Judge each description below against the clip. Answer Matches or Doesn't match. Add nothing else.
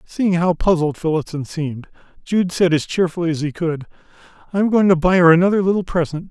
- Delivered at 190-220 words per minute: Matches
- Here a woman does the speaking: Doesn't match